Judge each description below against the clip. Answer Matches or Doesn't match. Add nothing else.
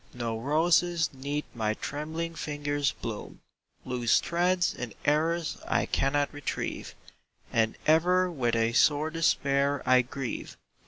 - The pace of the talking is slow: Matches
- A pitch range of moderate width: Matches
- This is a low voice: Doesn't match